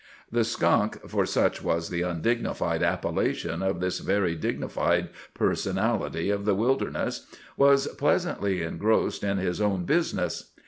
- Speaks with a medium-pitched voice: No, low, 100 Hz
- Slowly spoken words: Yes, slow, 120 wpm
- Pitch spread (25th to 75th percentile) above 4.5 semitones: No, average, 4.0 semitones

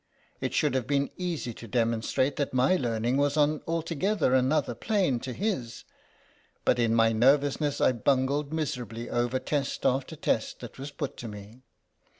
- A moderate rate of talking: Yes, average, 170 wpm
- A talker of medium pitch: No, low, 130 Hz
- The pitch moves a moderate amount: Yes, average, 3.7 semitones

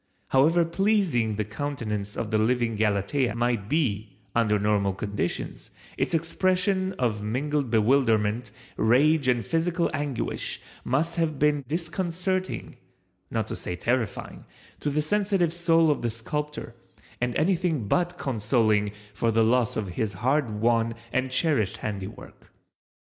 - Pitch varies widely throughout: Yes, wide, 6.9 semitones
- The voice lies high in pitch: No, low, 125 Hz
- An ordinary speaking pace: No, slow, 130 wpm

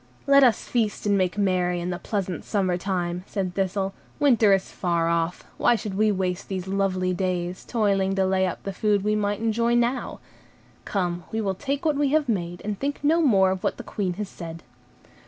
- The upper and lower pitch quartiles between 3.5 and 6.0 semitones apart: No, average, 3.1 semitones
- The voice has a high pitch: Yes, high, 195 Hz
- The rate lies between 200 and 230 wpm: Yes, fast, 205 wpm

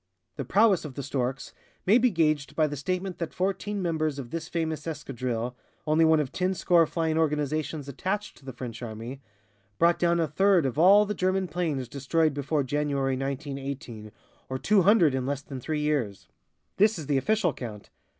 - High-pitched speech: No, medium, 150 Hz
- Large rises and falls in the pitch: No, average, 4.4 semitones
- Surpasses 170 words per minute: Yes, average, 185 wpm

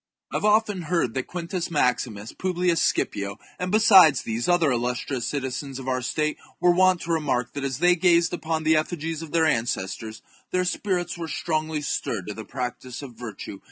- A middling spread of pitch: No, wide, 5.9 semitones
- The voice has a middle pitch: Yes, medium, 155 Hz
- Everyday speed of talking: Yes, average, 185 wpm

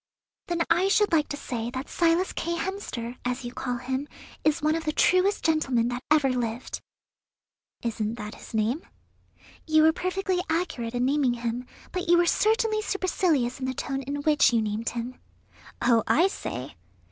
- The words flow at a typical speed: Yes, average, 175 wpm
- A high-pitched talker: Yes, very high, 280 Hz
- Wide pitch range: Yes, wide, 5.9 semitones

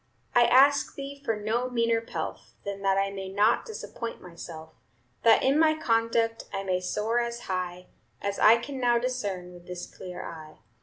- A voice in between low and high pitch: No, high, 225 Hz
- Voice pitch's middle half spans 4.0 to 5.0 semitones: Yes, average, 4.5 semitones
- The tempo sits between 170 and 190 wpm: Yes, average, 175 wpm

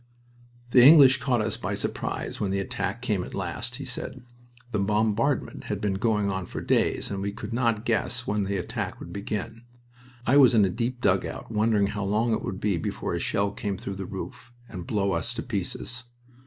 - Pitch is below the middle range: Yes, low, 105 Hz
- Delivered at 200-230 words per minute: Yes, fast, 205 wpm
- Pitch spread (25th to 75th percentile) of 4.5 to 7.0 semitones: No, average, 3.2 semitones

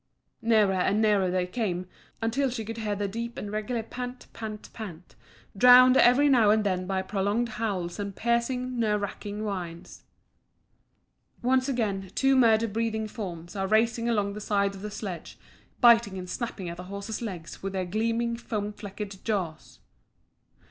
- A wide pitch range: No, average, 3.3 semitones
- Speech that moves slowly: No, average, 165 wpm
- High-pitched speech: Yes, high, 210 Hz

